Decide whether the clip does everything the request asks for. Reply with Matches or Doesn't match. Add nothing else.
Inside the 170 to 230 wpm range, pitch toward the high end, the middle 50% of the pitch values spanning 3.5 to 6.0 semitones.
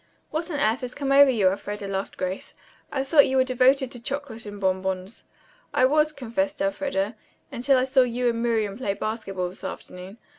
Matches